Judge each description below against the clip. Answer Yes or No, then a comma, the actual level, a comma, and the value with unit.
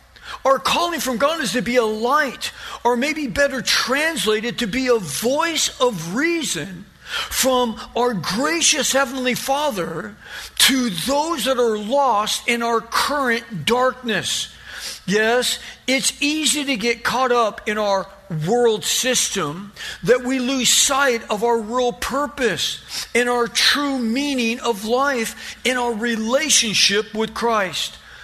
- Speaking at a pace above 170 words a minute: No, slow, 135 wpm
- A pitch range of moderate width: Yes, average, 3.3 semitones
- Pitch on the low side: No, high, 245 Hz